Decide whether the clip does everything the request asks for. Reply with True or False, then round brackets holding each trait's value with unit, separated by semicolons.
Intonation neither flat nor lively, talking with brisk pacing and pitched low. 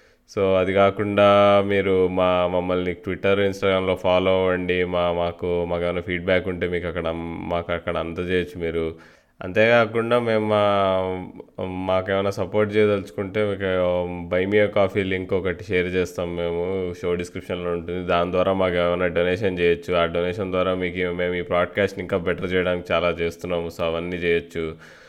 False (1.6 semitones; 145 wpm; 90 Hz)